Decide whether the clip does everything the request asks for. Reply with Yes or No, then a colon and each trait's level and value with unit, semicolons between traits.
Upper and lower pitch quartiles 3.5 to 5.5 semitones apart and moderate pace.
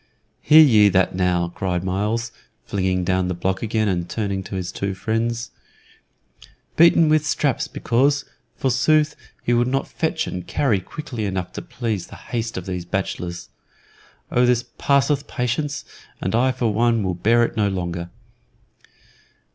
Yes: average, 5.0 semitones; average, 155 wpm